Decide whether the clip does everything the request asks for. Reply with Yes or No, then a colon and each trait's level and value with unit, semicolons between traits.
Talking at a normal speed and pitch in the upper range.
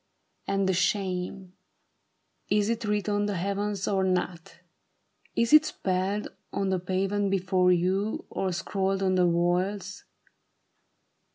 No: slow, 125 wpm; high, 195 Hz